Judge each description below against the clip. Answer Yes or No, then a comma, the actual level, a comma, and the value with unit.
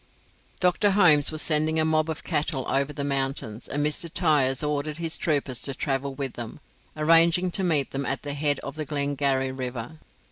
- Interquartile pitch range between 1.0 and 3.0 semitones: Yes, narrow, 2.6 semitones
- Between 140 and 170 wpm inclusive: No, average, 185 wpm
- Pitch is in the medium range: Yes, medium, 145 Hz